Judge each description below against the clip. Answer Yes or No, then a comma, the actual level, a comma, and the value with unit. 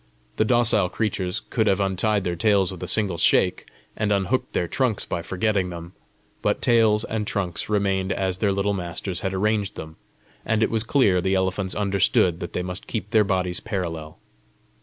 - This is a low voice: Yes, very low, 95 Hz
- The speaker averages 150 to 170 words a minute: No, average, 180 wpm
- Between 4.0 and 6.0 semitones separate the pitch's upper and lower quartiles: No, average, 2.8 semitones